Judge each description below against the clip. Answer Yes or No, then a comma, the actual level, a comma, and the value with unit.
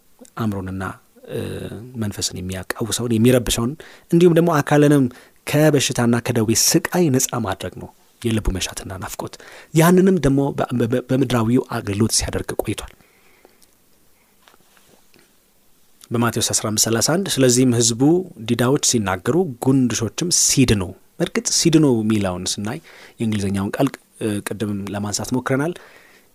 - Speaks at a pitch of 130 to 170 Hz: No, low, 120 Hz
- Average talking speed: Yes, average, 90 wpm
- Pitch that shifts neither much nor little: Yes, average, 4.7 semitones